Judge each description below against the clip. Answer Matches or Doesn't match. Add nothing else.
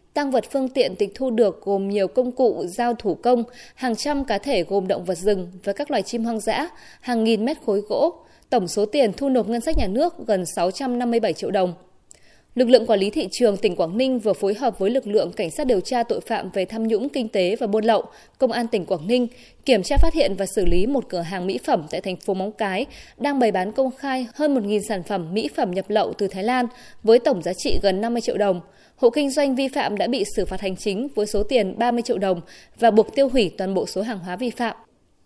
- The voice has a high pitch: Matches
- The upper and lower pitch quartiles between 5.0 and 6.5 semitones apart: Doesn't match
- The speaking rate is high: Matches